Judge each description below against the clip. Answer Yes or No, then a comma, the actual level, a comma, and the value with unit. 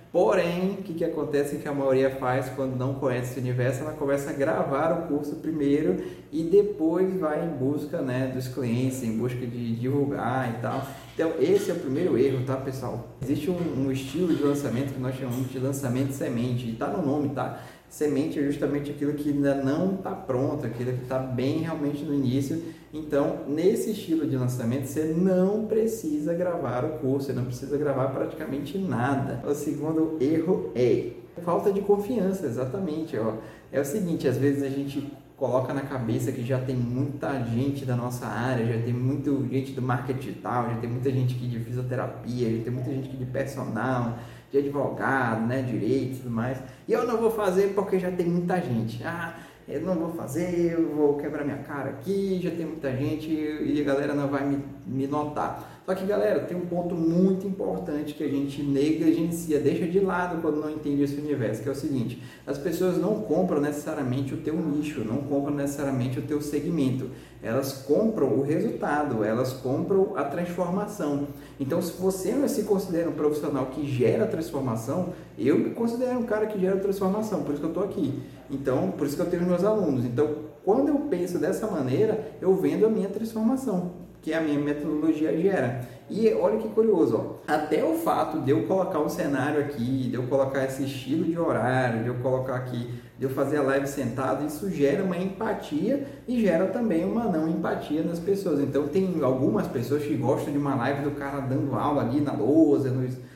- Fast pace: Yes, fast, 195 wpm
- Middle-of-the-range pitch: Yes, medium, 145 Hz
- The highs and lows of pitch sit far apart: No, average, 4.1 semitones